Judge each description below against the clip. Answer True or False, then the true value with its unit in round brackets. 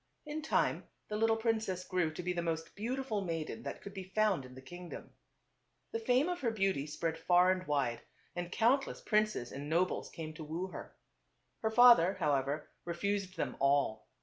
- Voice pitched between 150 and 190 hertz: True (185 Hz)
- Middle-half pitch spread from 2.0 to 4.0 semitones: False (5.5 semitones)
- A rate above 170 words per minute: True (185 wpm)